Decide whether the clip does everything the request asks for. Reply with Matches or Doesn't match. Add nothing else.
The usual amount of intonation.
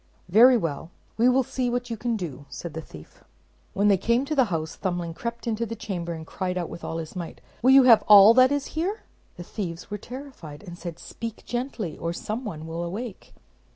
Doesn't match